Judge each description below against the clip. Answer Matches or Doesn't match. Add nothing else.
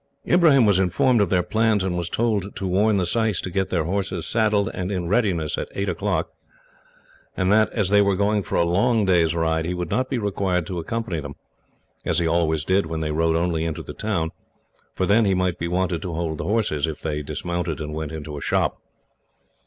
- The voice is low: Matches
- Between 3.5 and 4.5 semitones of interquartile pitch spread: Matches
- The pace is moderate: Doesn't match